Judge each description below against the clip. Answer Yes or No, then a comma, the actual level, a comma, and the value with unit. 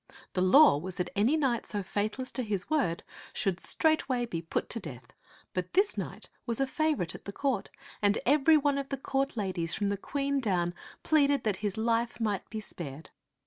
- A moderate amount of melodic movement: No, wide, 6.7 semitones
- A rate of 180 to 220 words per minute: Yes, average, 195 wpm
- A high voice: Yes, high, 225 Hz